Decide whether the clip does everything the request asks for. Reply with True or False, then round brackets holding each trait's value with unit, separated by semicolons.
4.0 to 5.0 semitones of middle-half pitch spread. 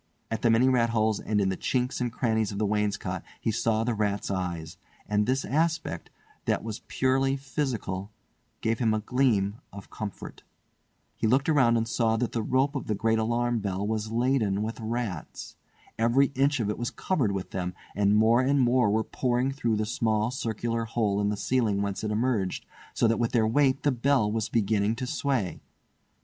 False (3.2 semitones)